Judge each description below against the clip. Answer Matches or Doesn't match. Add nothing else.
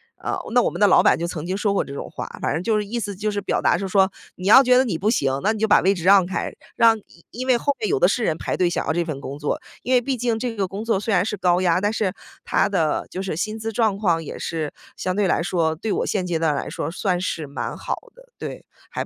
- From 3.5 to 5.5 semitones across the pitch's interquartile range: Matches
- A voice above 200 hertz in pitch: Doesn't match